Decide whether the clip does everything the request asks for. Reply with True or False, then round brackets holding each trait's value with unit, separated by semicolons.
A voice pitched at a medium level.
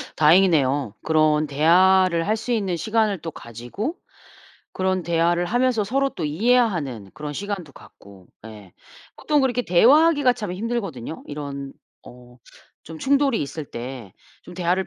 True (175 Hz)